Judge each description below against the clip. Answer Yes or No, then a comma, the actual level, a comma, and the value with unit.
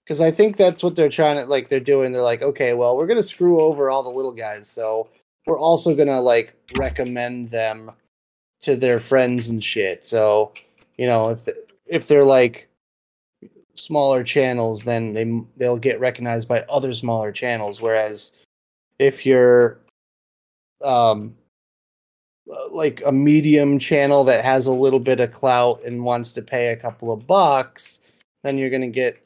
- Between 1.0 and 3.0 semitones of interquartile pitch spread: No, average, 3.4 semitones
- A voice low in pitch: Yes, low, 125 Hz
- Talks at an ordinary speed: Yes, average, 170 wpm